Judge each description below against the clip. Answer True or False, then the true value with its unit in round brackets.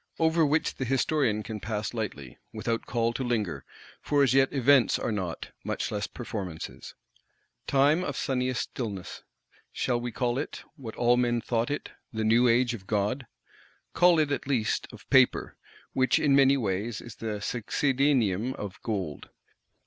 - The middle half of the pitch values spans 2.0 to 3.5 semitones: False (4.0 semitones)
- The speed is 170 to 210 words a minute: False (155 wpm)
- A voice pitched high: False (120 Hz)